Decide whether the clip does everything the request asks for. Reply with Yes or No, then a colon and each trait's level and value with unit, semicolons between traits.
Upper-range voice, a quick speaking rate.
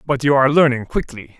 No: low, 130 Hz; fast, 215 wpm